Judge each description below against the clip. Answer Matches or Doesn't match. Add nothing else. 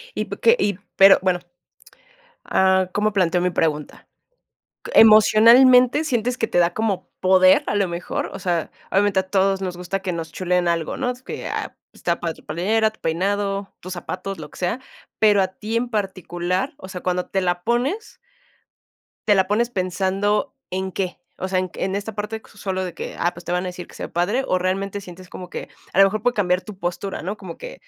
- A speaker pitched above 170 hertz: Matches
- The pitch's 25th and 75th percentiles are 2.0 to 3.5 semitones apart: Matches